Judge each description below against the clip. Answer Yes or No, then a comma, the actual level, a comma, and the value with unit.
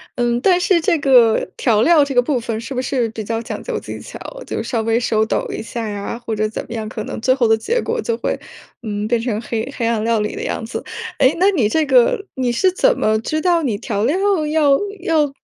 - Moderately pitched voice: No, high, 240 Hz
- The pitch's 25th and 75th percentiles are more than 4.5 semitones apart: Yes, average, 5.1 semitones